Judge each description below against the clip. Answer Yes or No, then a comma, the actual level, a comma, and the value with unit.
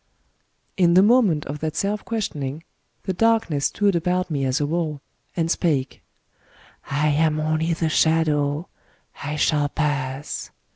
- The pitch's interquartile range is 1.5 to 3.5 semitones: Yes, average, 3.1 semitones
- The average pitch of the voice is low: No, medium, 155 Hz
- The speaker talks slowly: No, average, 155 wpm